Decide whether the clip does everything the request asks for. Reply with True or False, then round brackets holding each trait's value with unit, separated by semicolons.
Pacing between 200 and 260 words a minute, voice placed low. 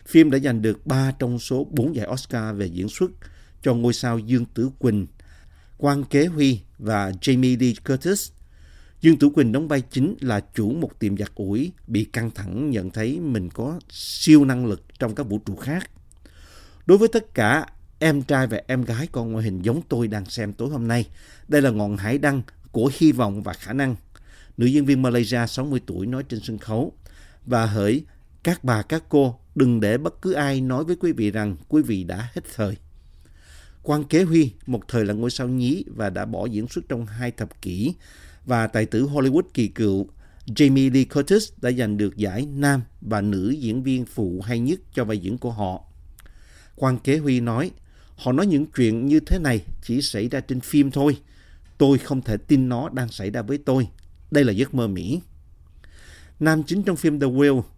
True (205 wpm; 120 Hz)